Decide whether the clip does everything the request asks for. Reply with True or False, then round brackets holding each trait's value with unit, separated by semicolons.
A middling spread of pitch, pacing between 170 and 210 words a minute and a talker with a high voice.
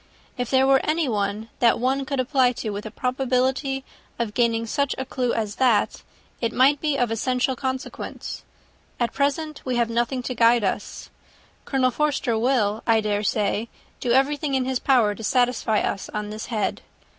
True (3.0 semitones; 175 wpm; 250 Hz)